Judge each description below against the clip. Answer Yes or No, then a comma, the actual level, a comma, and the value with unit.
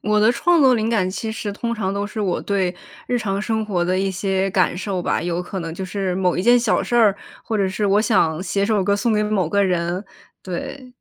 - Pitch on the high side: Yes, high, 200 Hz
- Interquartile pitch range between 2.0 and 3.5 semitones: Yes, average, 2.9 semitones